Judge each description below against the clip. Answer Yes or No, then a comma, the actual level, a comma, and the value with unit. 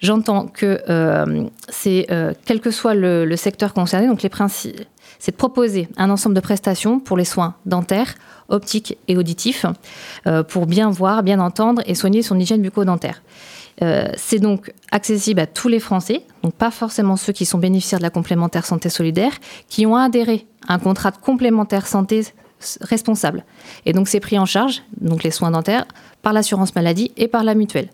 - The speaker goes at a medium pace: Yes, average, 185 wpm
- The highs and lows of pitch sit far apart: No, average, 3.4 semitones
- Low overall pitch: No, high, 200 Hz